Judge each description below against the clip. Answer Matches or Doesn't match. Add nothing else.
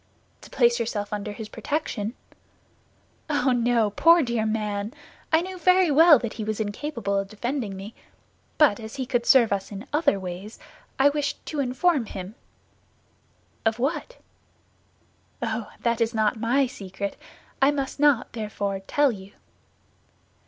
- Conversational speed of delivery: Matches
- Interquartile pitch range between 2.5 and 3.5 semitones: Doesn't match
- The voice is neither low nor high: Doesn't match